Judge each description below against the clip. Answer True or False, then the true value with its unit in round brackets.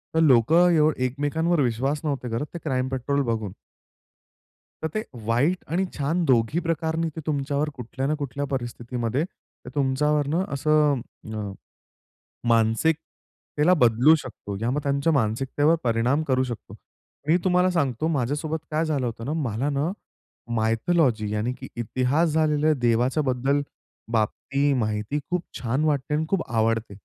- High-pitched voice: False (140 Hz)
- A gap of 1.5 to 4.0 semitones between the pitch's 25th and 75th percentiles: False (4.6 semitones)